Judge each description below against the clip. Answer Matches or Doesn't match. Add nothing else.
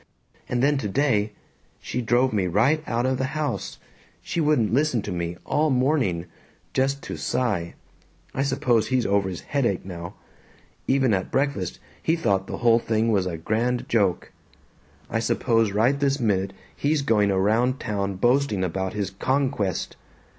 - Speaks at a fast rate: Doesn't match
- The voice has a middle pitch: Doesn't match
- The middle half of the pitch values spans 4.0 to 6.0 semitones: Matches